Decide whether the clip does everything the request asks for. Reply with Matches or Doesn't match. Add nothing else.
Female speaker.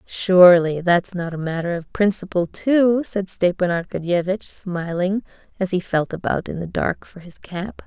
Matches